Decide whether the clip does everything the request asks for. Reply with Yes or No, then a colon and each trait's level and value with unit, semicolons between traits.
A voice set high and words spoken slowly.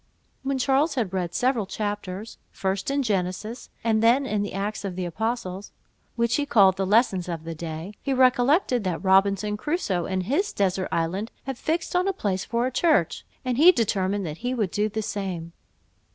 No: high, 210 Hz; average, 190 wpm